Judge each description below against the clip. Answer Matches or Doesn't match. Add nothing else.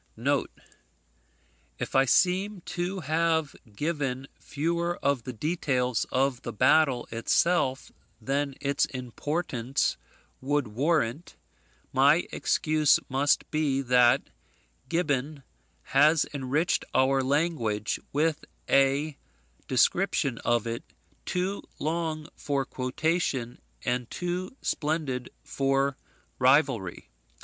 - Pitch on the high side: Doesn't match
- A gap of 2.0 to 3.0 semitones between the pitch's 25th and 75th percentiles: Doesn't match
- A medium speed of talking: Doesn't match